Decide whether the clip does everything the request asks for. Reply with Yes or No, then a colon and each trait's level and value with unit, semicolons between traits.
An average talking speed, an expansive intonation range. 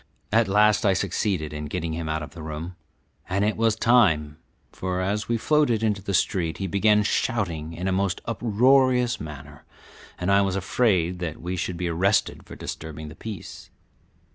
No: average, 180 wpm; average, 4.6 semitones